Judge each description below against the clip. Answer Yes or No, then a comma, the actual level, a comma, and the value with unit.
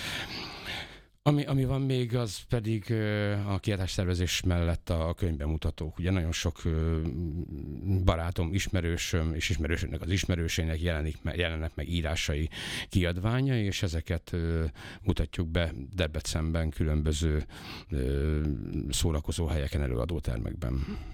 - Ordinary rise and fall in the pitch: Yes, average, 3.0 semitones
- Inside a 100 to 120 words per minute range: Yes, average, 115 wpm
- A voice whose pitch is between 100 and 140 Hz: No, very low, 85 Hz